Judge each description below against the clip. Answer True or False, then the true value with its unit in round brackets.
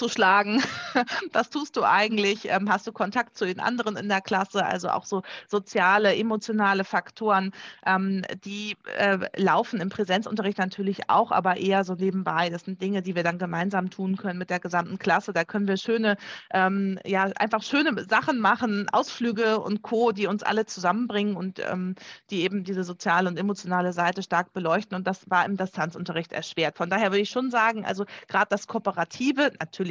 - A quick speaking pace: False (175 wpm)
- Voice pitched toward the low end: False (195 Hz)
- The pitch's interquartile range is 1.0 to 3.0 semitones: True (2.7 semitones)